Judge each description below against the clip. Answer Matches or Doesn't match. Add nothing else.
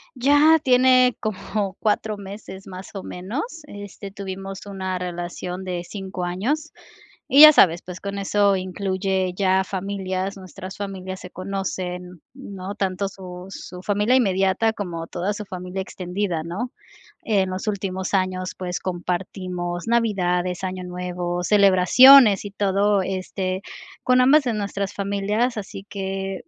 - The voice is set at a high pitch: Matches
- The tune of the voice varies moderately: Doesn't match